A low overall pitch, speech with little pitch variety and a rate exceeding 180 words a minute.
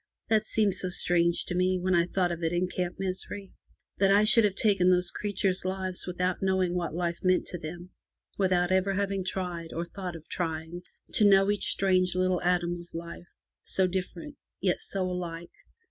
No: medium, 185 Hz; narrow, 1.6 semitones; average, 190 wpm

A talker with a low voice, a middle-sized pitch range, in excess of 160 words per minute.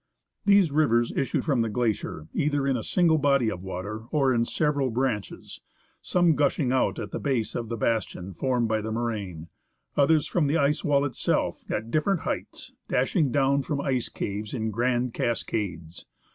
Yes: low, 125 Hz; average, 4.6 semitones; average, 175 wpm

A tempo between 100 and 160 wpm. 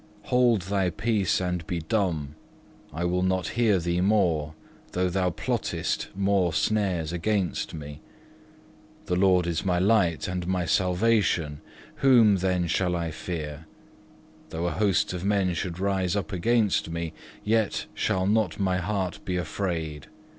Yes: average, 145 wpm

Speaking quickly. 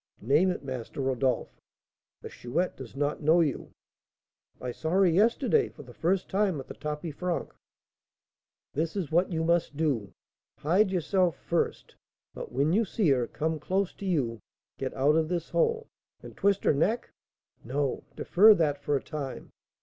No: average, 170 wpm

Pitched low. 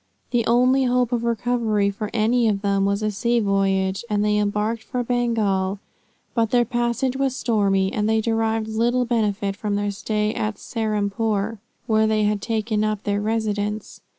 No: high, 215 Hz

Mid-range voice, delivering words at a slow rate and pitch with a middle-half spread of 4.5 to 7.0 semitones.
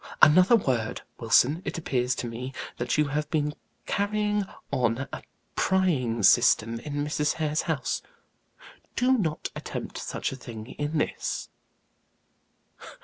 Yes: medium, 145 Hz; slow, 130 wpm; average, 4.9 semitones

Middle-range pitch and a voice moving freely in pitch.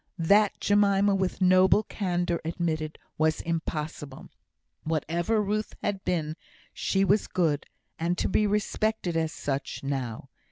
No: medium, 175 Hz; average, 4.2 semitones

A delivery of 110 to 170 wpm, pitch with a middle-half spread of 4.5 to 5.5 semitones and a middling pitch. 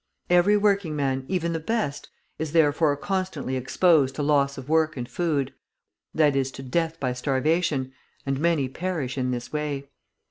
No: average, 165 wpm; average, 3.9 semitones; medium, 150 Hz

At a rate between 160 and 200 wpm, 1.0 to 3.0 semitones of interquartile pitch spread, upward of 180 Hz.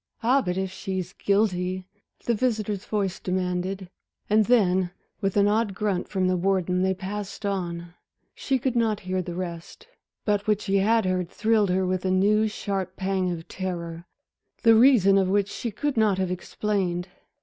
Yes: average, 170 wpm; narrow, 2.5 semitones; high, 190 Hz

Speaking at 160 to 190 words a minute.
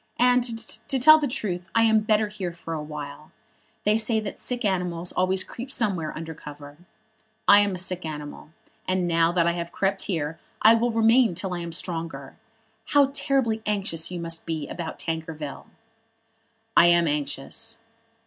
Yes: average, 170 wpm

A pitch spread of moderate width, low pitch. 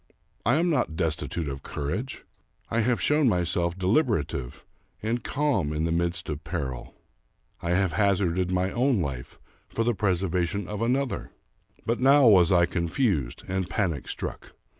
No: wide, 5.8 semitones; very low, 95 Hz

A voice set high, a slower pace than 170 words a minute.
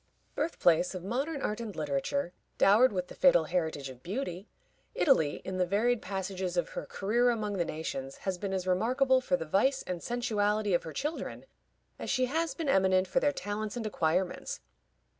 No: high, 200 Hz; average, 185 wpm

